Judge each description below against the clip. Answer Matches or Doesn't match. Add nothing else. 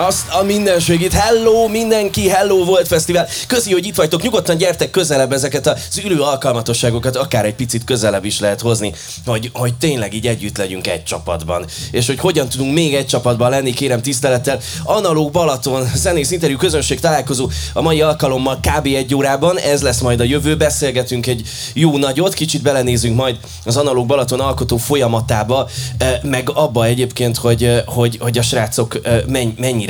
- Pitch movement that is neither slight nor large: Matches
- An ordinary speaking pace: Doesn't match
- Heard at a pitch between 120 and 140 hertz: Matches